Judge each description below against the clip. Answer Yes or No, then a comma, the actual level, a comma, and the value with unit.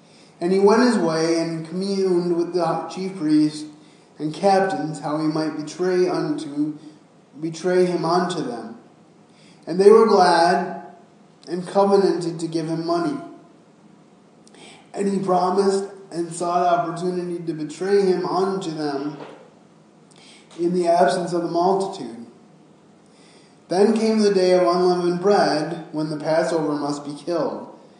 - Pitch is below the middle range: No, medium, 175 Hz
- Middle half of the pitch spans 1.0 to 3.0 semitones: Yes, average, 2.7 semitones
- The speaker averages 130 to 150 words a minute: Yes, slow, 135 wpm